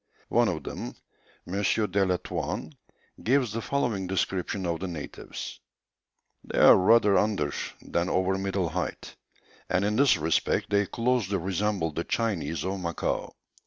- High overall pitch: No, very low, 95 Hz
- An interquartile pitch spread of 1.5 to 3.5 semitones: Yes, average, 3.1 semitones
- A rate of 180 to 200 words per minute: No, average, 145 wpm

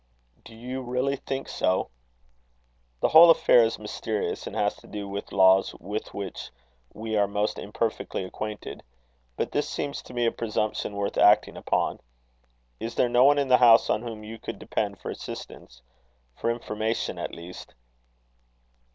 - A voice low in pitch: Yes, low, 110 Hz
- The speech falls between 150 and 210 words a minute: Yes, average, 160 wpm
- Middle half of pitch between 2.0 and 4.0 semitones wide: Yes, average, 3.0 semitones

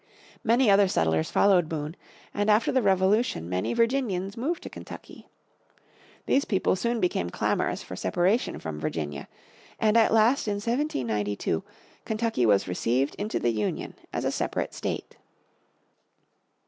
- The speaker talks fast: No, slow, 135 wpm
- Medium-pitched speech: No, high, 195 Hz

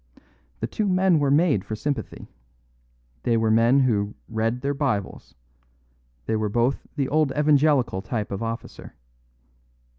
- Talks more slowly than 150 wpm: Yes, average, 140 wpm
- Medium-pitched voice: No, low, 125 Hz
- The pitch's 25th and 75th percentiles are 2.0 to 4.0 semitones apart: No, average, 4.7 semitones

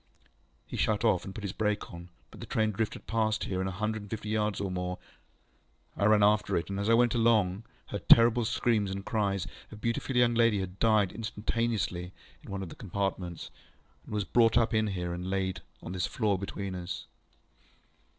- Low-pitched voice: Yes, low, 105 Hz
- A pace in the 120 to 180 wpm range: No, average, 200 wpm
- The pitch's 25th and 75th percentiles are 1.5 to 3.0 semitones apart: Yes, average, 2.7 semitones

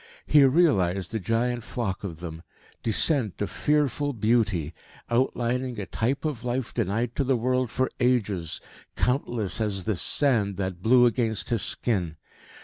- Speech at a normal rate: Yes, average, 145 wpm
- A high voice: No, low, 115 Hz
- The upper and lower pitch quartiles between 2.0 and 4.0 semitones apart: No, average, 4.4 semitones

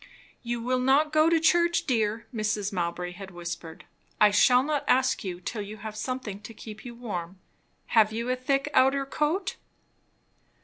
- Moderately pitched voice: No, high, 230 Hz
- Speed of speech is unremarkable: Yes, average, 170 wpm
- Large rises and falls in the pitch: No, average, 4.7 semitones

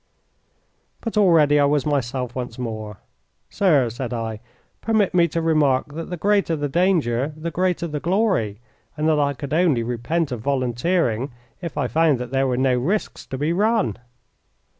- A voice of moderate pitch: Yes, medium, 145 Hz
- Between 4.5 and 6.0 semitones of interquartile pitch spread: Yes, wide, 5.4 semitones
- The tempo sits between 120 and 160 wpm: No, average, 170 wpm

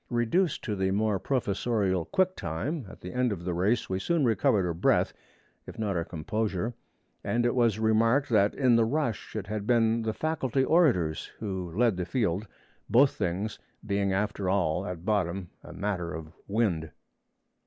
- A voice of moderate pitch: No, low, 105 Hz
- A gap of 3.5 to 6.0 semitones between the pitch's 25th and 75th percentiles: Yes, average, 4.5 semitones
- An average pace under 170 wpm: No, average, 175 wpm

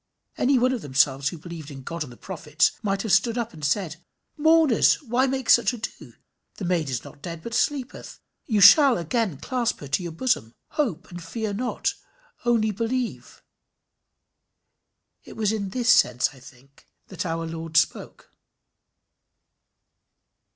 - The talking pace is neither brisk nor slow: Yes, average, 160 wpm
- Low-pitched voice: No, high, 195 Hz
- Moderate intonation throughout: No, wide, 7.2 semitones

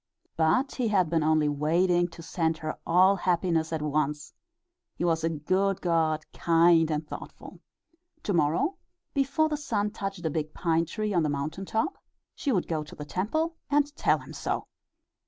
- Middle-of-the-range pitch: Yes, medium, 170 Hz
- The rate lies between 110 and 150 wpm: No, average, 175 wpm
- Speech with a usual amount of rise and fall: Yes, average, 4.2 semitones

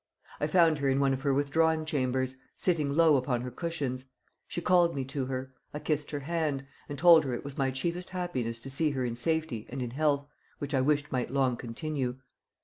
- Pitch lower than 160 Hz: Yes, medium, 140 Hz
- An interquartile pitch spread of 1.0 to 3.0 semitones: No, average, 3.4 semitones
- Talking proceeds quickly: Yes, fast, 215 wpm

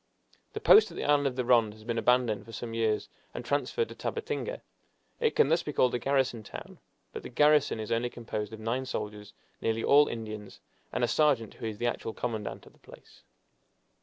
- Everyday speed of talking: No, fast, 210 wpm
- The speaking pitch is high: No, low, 120 Hz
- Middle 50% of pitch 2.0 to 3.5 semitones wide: No, average, 3.9 semitones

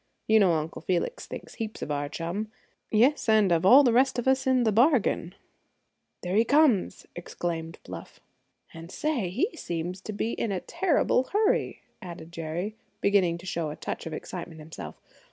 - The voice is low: No, high, 195 Hz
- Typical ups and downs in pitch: No, wide, 6.3 semitones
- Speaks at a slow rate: No, average, 175 wpm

